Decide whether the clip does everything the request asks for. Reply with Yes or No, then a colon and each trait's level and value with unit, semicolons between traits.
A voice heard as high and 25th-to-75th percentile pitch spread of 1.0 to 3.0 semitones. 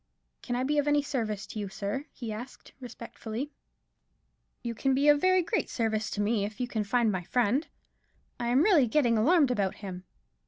No: high, 240 Hz; average, 4.8 semitones